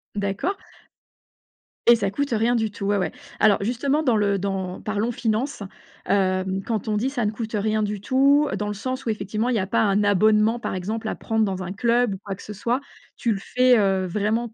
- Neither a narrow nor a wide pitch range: Yes, average, 3.1 semitones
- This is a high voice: Yes, high, 215 Hz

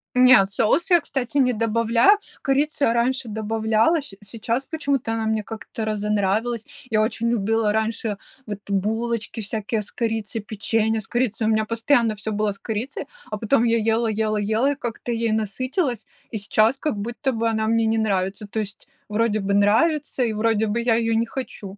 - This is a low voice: No, high, 225 Hz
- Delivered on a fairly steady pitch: Yes, narrow, 1.9 semitones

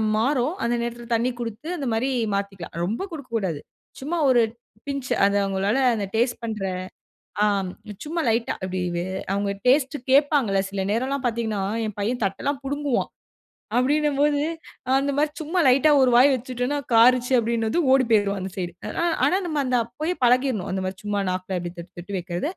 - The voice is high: Yes, high, 240 Hz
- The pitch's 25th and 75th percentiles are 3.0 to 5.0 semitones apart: No, wide, 5.6 semitones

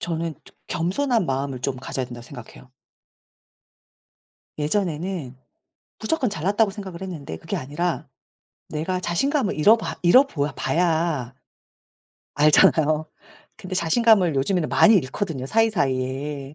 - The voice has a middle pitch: Yes, medium, 165 Hz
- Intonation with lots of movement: Yes, wide, 5.7 semitones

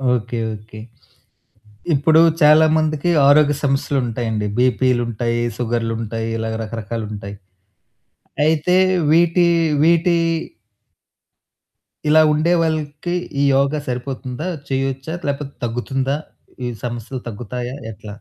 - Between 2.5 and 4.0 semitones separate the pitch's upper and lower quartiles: No, average, 4.5 semitones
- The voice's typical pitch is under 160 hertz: Yes, low, 135 Hz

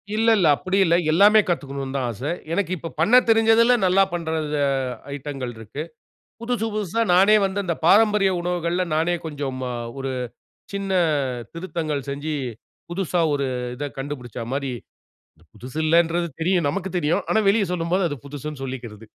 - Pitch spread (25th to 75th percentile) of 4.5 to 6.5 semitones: Yes, wide, 5.4 semitones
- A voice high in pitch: No, medium, 165 Hz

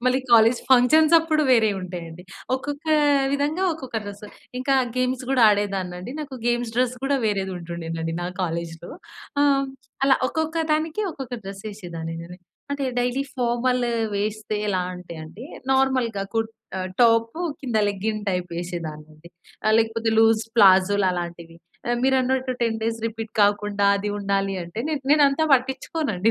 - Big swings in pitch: Yes, wide, 5.8 semitones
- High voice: Yes, high, 225 Hz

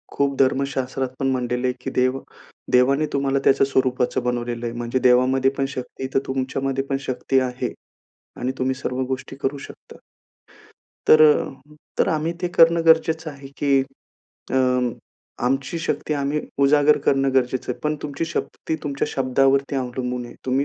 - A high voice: No, low, 135 Hz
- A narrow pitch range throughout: Yes, narrow, 1.6 semitones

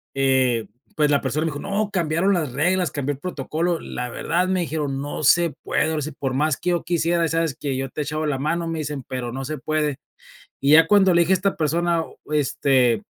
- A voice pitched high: No, medium, 155 Hz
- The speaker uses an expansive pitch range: No, average, 3.7 semitones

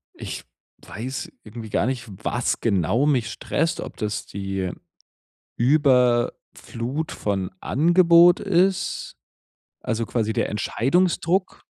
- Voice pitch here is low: Yes, low, 125 Hz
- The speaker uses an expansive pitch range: Yes, wide, 7.0 semitones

